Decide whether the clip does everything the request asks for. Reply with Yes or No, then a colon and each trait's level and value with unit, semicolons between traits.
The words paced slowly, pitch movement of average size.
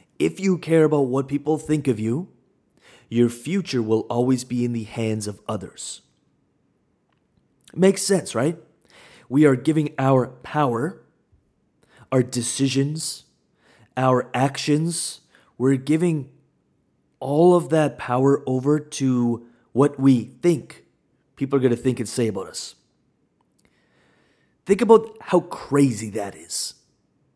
Yes: slow, 125 wpm; average, 4.2 semitones